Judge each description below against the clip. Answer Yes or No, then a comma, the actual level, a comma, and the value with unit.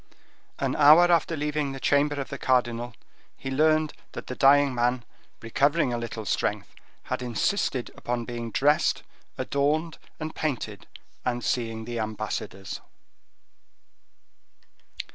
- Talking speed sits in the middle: No, slow, 125 wpm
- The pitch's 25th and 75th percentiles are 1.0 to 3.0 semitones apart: No, average, 3.9 semitones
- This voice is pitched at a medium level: No, low, 130 Hz